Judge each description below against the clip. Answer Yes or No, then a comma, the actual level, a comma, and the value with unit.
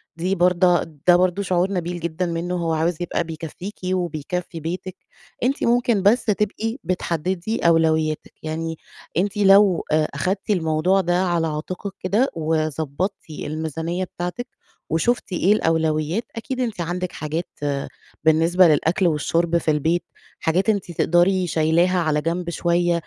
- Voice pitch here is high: No, medium, 175 Hz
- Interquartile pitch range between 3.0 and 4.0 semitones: No, narrow, 2.6 semitones